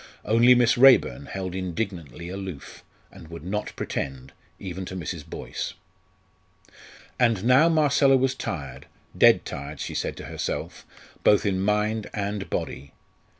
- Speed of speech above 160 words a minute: No, slow, 135 wpm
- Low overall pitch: Yes, very low, 95 Hz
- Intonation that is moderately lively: No, wide, 5.8 semitones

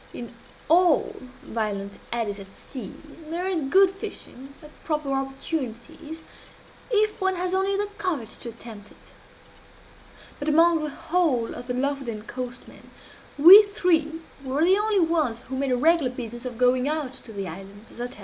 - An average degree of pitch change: No, wide, 6.1 semitones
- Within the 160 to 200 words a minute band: Yes, average, 170 wpm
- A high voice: Yes, very high, 275 Hz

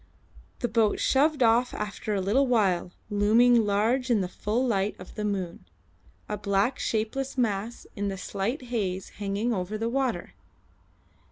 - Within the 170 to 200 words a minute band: No, average, 155 wpm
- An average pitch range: Yes, average, 3.3 semitones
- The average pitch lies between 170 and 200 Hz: No, high, 215 Hz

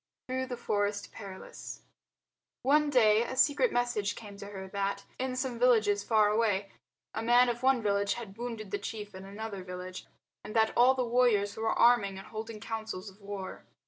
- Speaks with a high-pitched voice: Yes, high, 220 Hz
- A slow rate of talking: No, average, 180 wpm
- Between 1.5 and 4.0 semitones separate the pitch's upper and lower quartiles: Yes, average, 3.3 semitones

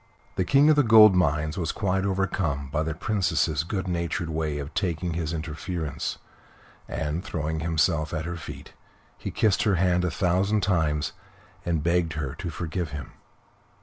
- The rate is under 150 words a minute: No, average, 165 wpm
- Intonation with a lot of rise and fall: No, average, 3.1 semitones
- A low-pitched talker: Yes, very low, 85 Hz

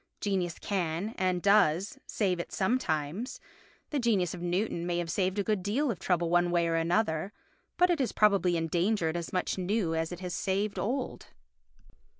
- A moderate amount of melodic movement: Yes, average, 3.5 semitones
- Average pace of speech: Yes, average, 175 wpm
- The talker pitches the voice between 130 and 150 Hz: No, medium, 185 Hz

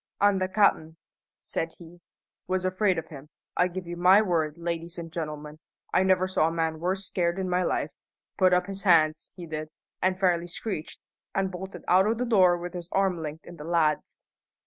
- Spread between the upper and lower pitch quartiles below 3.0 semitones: Yes, narrow, 2.4 semitones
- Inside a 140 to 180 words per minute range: No, average, 200 wpm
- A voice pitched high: No, medium, 175 Hz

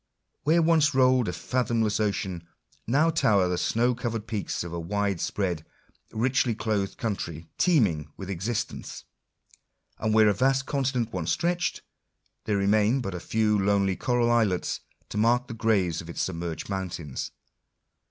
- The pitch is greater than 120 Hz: No, low, 110 Hz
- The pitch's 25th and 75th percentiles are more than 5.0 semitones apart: No, average, 4.5 semitones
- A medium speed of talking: Yes, average, 155 wpm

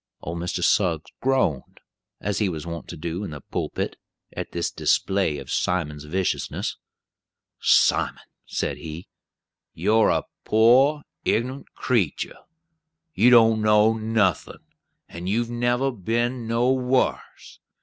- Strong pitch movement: Yes, wide, 5.7 semitones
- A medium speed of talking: No, slow, 120 wpm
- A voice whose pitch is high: No, low, 110 Hz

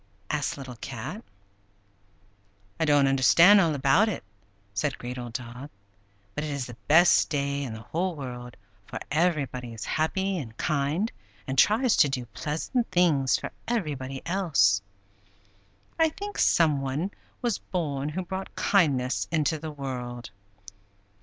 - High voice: No, medium, 145 Hz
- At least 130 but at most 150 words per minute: Yes, average, 140 wpm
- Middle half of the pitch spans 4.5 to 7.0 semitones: Yes, average, 5.3 semitones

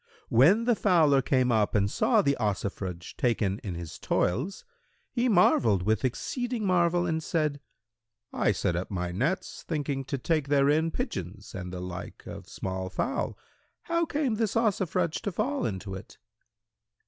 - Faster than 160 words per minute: No, average, 155 wpm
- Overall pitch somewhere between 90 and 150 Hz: Yes, medium, 140 Hz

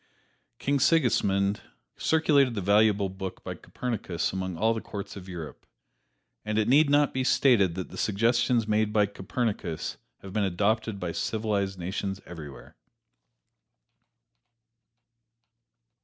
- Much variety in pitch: No, average, 3.5 semitones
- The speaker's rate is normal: No, slow, 125 wpm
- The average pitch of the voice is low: Yes, low, 105 Hz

